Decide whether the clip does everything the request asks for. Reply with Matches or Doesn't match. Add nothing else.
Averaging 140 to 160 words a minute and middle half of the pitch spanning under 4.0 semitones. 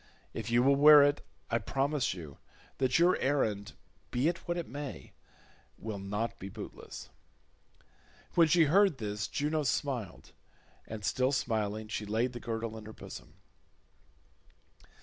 Doesn't match